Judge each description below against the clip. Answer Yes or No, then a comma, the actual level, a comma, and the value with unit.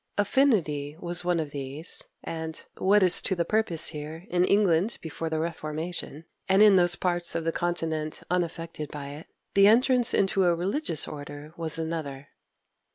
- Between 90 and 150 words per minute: No, average, 160 wpm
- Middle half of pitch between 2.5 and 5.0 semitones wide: Yes, average, 3.1 semitones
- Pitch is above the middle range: No, medium, 165 Hz